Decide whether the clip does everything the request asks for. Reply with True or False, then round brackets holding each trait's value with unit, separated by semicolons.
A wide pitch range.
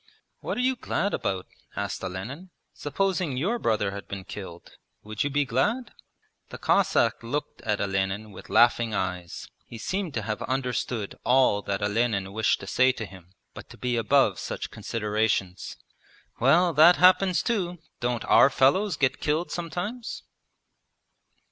True (8.6 semitones)